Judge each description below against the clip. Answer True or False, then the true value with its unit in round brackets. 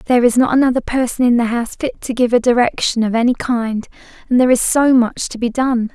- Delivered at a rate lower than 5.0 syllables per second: False (6.0 syllables/s)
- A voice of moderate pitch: False (245 Hz)